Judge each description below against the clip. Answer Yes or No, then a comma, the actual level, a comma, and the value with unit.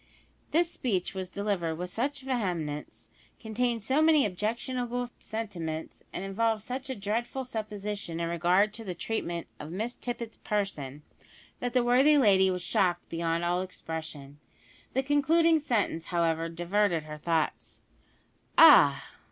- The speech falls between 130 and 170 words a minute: Yes, slow, 135 wpm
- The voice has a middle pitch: No, high, 205 Hz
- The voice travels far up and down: Yes, wide, 6.1 semitones